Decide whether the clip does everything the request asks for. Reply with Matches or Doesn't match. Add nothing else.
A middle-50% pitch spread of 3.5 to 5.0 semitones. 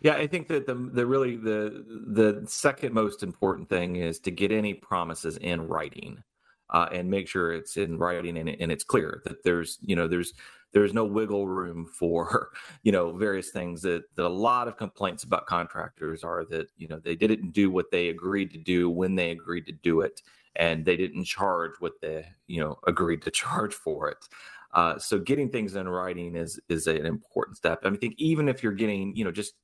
Matches